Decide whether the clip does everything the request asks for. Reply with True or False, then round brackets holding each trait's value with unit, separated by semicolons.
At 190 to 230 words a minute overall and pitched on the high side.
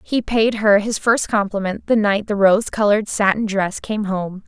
True (200 wpm; 205 Hz)